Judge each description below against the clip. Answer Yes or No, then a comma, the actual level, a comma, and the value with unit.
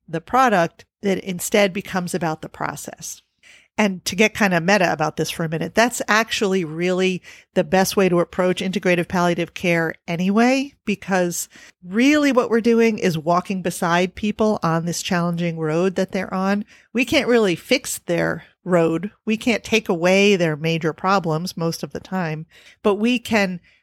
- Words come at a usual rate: Yes, average, 170 wpm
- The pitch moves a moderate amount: Yes, average, 3.8 semitones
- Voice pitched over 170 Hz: Yes, medium, 185 Hz